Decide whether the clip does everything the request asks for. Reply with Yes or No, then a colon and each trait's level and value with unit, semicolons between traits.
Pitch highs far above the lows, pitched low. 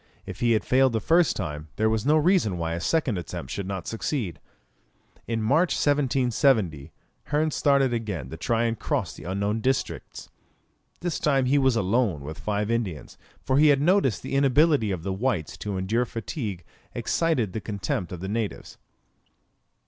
Yes: wide, 6.3 semitones; low, 115 Hz